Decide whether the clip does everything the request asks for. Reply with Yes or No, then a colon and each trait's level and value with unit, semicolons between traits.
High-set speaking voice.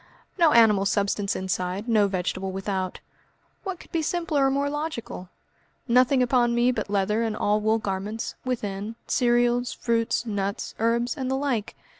Yes: high, 230 Hz